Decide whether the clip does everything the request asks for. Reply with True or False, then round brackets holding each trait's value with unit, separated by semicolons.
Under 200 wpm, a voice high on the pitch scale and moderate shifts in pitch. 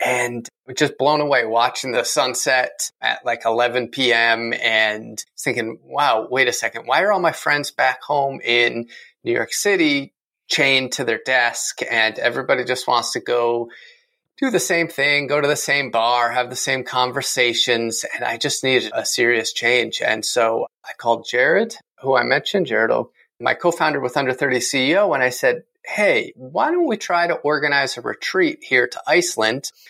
False (180 wpm; 130 Hz; 3.9 semitones)